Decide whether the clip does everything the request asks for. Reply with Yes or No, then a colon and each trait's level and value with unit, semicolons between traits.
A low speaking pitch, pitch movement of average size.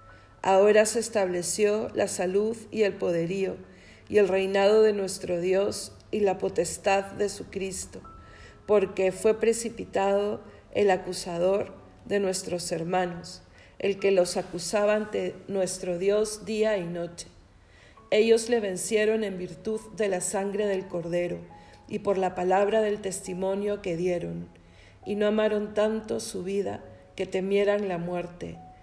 No: high, 190 Hz; average, 3.1 semitones